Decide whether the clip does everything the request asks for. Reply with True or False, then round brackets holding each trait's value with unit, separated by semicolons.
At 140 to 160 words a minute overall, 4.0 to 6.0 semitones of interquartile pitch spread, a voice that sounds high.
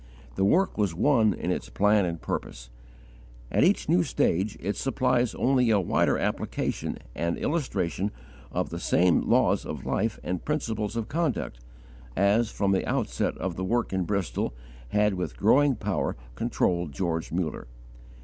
False (155 wpm; 4.8 semitones; 100 Hz)